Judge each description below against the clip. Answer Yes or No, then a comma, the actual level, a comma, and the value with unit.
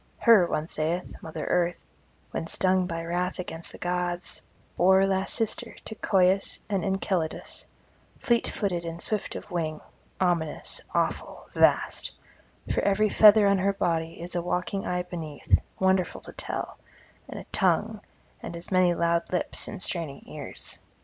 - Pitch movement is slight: Yes, narrow, 2.3 semitones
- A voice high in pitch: No, medium, 180 Hz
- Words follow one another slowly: No, average, 150 wpm